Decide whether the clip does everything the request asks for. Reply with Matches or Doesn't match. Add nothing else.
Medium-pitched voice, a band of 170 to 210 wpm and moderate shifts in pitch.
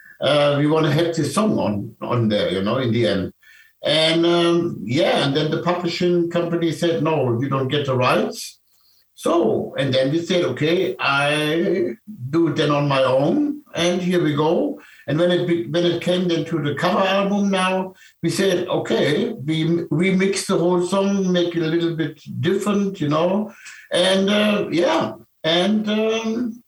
Matches